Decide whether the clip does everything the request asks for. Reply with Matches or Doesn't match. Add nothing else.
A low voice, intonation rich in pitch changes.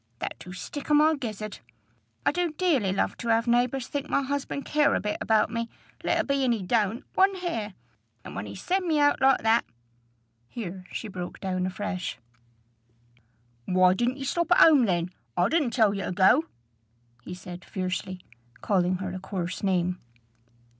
Doesn't match